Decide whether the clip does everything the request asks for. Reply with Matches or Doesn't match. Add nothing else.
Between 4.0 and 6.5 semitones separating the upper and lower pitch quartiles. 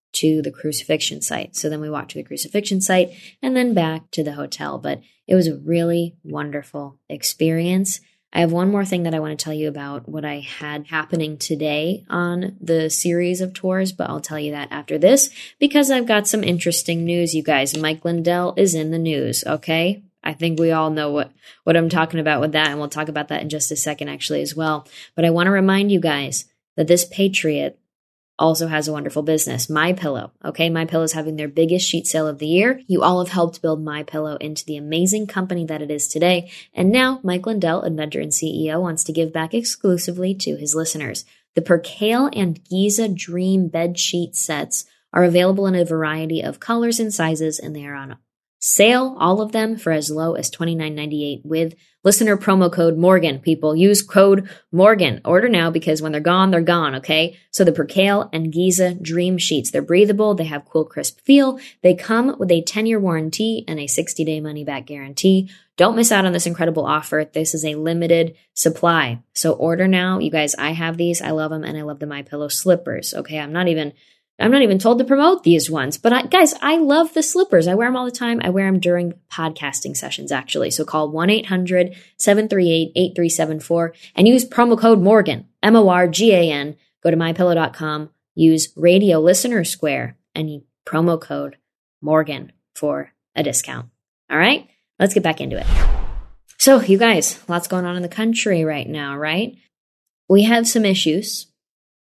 Doesn't match